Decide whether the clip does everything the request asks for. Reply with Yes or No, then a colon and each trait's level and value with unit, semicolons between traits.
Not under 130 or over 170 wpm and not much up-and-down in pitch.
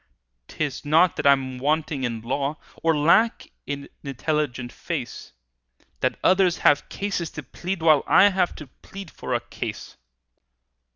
No: average, 140 wpm; average, 3.9 semitones